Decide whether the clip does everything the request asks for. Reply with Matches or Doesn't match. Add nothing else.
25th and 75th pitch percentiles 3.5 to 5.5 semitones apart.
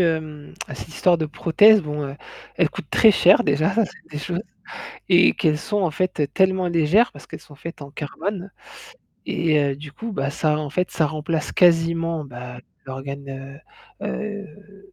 Matches